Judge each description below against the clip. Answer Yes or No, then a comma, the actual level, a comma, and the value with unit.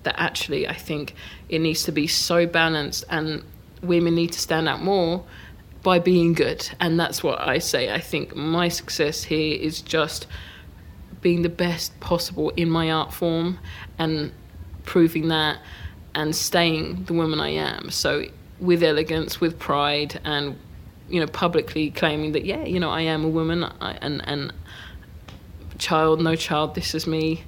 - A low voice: No, medium, 160 Hz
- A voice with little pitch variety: Yes, narrow, 2.3 semitones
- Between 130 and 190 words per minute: Yes, average, 165 wpm